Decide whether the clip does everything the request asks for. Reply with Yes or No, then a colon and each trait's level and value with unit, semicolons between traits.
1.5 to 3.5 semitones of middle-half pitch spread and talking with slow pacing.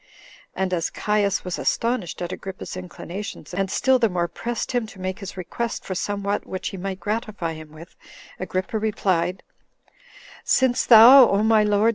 No: average, 3.1 semitones; average, 165 wpm